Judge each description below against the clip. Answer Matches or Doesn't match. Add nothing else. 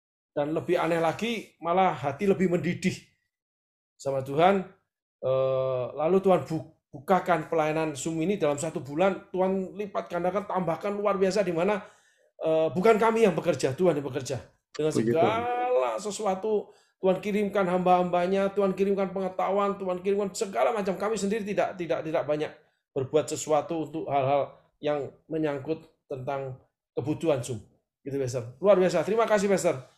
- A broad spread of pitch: Doesn't match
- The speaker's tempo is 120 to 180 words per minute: Matches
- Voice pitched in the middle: Matches